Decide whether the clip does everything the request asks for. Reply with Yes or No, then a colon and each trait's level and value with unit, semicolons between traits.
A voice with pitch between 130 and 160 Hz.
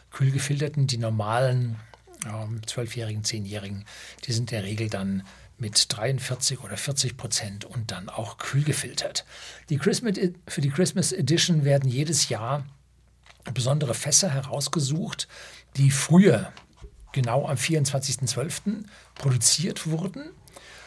Yes: low, 135 Hz